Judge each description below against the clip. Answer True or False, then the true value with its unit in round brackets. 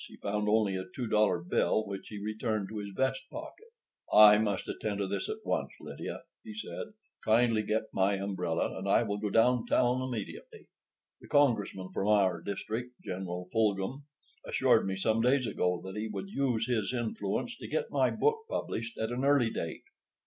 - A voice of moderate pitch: False (110 Hz)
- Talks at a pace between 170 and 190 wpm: True (185 wpm)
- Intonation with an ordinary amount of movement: True (4.0 semitones)